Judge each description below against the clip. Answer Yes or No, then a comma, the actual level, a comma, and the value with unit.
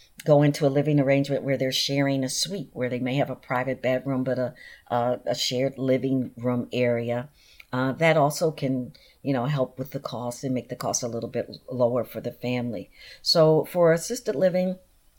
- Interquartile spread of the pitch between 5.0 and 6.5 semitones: No, average, 2.7 semitones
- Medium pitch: No, low, 130 Hz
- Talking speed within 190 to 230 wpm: Yes, average, 200 wpm